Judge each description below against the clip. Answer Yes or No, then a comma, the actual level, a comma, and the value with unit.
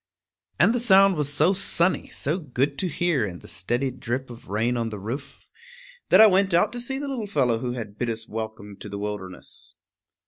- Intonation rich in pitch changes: Yes, wide, 8.7 semitones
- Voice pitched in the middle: No, low, 130 Hz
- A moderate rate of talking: No, fast, 215 wpm